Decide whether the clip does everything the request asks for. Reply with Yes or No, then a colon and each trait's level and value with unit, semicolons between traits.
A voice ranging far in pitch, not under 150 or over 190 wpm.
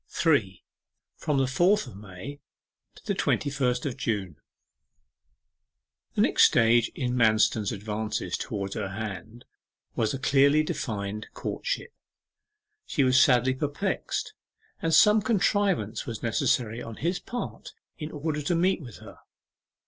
No: wide, 5.9 semitones; slow, 135 wpm